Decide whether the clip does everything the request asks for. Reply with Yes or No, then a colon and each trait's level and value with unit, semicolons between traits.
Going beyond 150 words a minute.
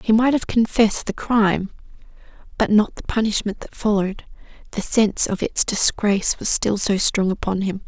Yes: average, 175 wpm